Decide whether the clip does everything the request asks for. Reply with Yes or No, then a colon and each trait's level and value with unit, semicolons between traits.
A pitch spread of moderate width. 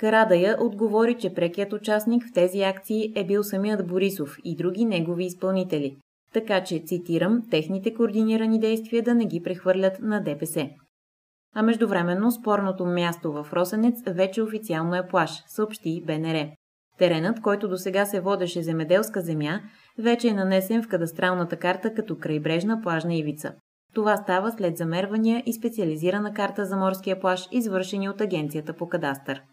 Yes: average, 4.2 semitones